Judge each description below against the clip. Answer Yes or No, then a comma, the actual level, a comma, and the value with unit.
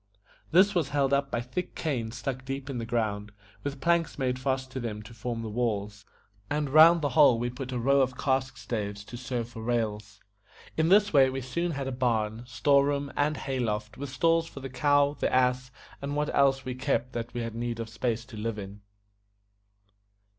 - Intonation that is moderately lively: Yes, average, 3.4 semitones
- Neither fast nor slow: No, fast, 210 wpm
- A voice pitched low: Yes, low, 130 Hz